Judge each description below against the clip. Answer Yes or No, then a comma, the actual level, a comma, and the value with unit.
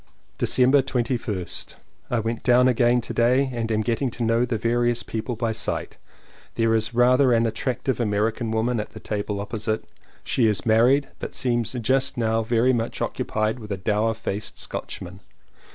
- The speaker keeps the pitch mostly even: Yes, narrow, 1.9 semitones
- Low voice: Yes, low, 115 Hz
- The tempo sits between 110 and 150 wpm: No, average, 170 wpm